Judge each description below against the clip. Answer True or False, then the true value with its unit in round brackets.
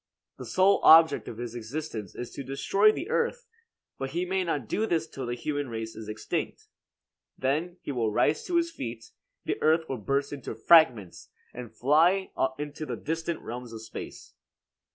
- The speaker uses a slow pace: False (175 wpm)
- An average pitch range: False (6.0 semitones)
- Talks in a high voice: False (145 Hz)